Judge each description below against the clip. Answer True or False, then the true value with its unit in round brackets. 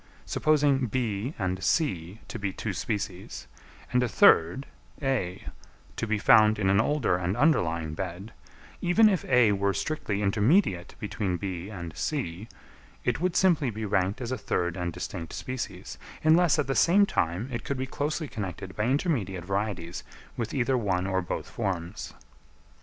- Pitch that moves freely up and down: True (6.3 semitones)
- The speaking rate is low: False (160 wpm)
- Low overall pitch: True (105 Hz)